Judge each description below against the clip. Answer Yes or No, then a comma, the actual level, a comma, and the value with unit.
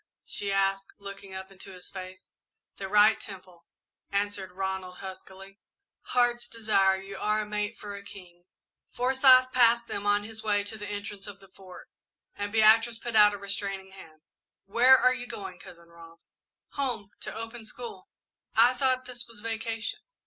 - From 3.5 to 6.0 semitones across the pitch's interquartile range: No, average, 2.9 semitones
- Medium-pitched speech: No, high, 205 Hz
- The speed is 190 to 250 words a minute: No, average, 165 wpm